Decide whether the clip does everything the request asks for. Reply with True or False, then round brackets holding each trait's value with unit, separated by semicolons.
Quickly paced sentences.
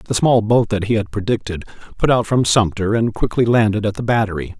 True (220 wpm)